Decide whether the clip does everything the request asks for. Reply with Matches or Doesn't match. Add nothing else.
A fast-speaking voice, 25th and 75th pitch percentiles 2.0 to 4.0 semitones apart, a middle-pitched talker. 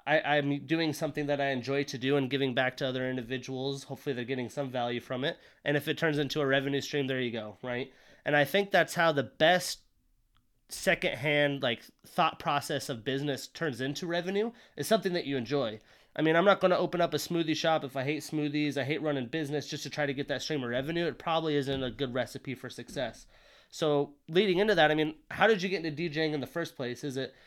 Matches